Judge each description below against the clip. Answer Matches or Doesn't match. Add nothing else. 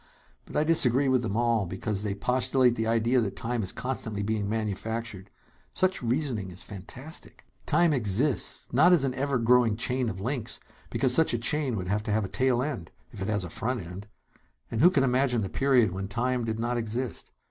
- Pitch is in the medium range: Doesn't match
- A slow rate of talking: Doesn't match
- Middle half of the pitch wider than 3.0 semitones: Matches